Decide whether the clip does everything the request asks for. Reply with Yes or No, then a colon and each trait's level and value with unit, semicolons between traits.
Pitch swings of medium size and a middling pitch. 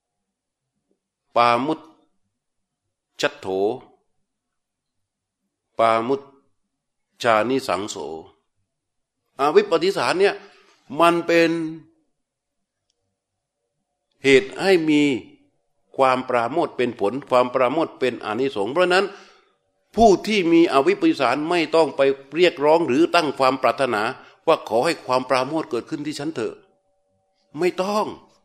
No: wide, 6.5 semitones; medium, 145 Hz